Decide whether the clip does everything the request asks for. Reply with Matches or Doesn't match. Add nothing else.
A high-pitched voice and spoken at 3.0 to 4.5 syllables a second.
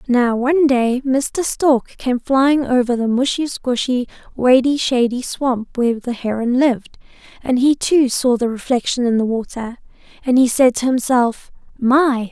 Matches